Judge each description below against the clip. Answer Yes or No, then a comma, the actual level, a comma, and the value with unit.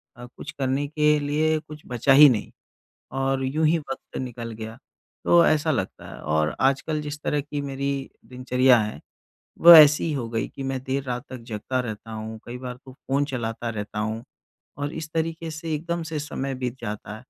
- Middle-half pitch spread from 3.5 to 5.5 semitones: Yes, average, 4.0 semitones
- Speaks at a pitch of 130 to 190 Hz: Yes, low, 135 Hz